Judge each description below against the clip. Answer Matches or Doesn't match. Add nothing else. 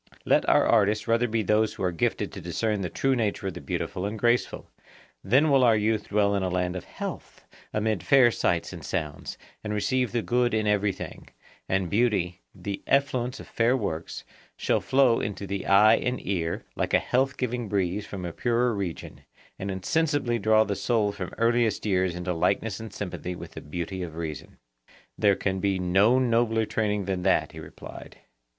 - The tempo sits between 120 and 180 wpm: Doesn't match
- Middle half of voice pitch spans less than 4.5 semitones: Matches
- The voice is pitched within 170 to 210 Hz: Doesn't match